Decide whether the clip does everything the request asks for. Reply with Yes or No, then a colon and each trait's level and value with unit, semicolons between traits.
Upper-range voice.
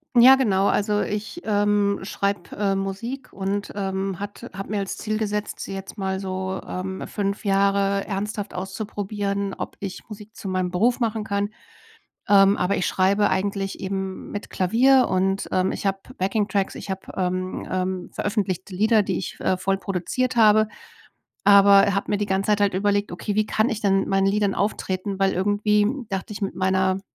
Yes: high, 200 Hz